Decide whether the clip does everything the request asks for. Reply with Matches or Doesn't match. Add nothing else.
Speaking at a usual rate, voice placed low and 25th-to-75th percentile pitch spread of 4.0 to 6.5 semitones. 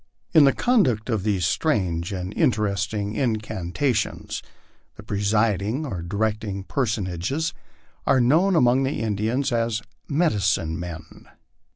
Doesn't match